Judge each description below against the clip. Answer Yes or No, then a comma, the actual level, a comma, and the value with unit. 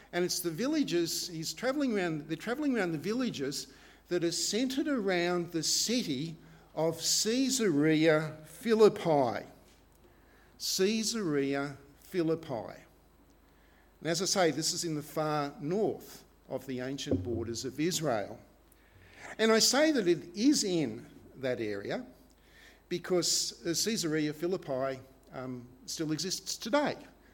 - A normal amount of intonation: No, wide, 6.0 semitones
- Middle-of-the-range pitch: Yes, medium, 165 Hz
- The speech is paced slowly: Yes, slow, 120 wpm